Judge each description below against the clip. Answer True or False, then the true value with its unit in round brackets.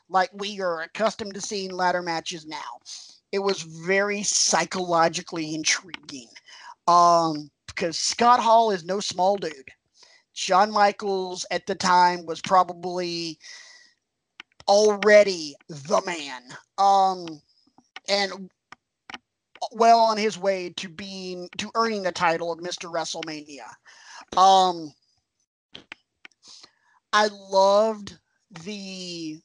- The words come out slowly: True (105 wpm)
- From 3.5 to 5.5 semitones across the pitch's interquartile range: False (3.1 semitones)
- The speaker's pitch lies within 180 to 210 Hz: True (185 Hz)